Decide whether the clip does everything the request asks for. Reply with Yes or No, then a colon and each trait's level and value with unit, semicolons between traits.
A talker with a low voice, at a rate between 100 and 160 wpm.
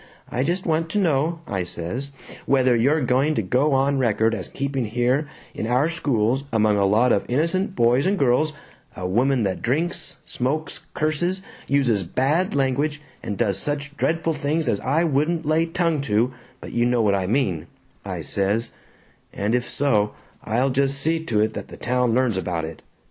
No: low, 130 Hz; average, 180 wpm